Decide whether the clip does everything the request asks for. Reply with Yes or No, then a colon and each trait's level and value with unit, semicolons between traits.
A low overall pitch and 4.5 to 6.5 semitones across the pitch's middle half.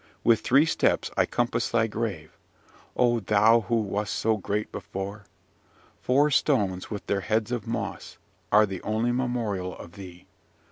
No: low, 110 Hz; average, 3.0 semitones